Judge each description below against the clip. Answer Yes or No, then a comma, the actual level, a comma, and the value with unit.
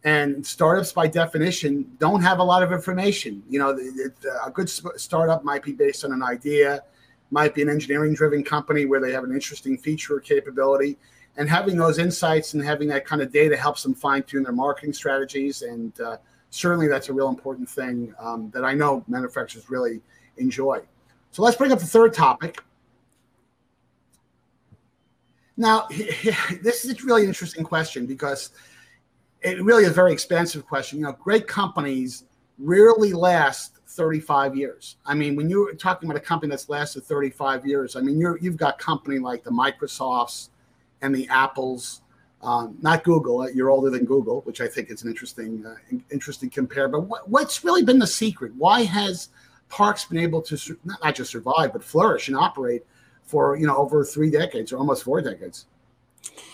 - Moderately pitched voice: Yes, medium, 145 Hz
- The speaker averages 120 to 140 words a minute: No, average, 180 wpm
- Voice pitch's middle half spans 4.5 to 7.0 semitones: Yes, average, 4.8 semitones